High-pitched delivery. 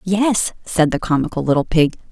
No: medium, 175 Hz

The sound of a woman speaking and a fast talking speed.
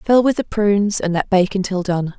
Yes: female; fast, 245 wpm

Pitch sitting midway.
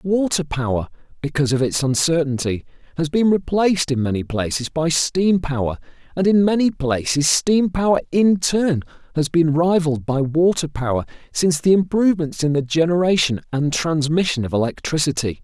Yes: medium, 155 Hz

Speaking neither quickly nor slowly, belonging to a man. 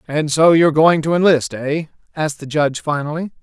Yes: average, 195 wpm; male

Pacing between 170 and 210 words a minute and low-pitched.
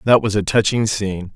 No: fast, 220 wpm; low, 105 Hz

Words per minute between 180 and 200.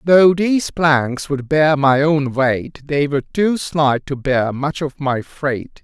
Yes: average, 185 wpm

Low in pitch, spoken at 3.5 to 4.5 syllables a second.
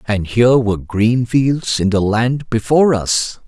Yes: low, 115 Hz; 4.2 syllables/s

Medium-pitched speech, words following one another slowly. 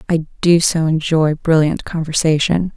Yes: medium, 160 Hz; slow, 130 wpm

